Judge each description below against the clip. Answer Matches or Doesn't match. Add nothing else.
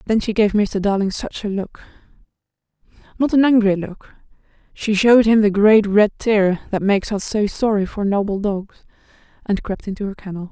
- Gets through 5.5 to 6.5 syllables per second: Doesn't match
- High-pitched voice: Matches